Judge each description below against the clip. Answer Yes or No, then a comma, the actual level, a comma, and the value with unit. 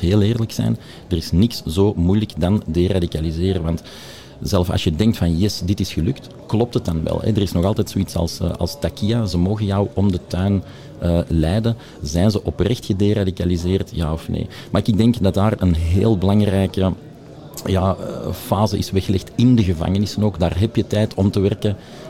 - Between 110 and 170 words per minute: No, average, 195 wpm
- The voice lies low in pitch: Yes, low, 100 Hz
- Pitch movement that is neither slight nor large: Yes, average, 3.5 semitones